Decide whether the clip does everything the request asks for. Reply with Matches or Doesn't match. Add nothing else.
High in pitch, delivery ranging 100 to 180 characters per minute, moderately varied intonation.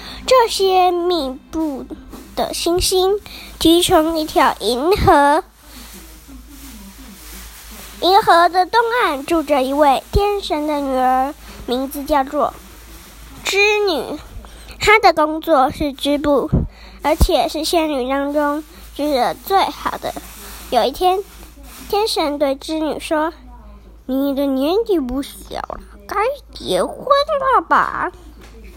Matches